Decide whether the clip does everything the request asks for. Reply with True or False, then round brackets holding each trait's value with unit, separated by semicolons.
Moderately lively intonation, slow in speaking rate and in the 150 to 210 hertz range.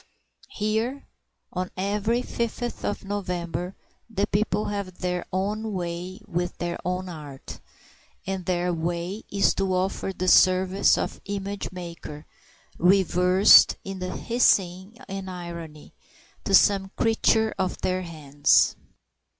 False (2.3 semitones; 120 wpm; 185 Hz)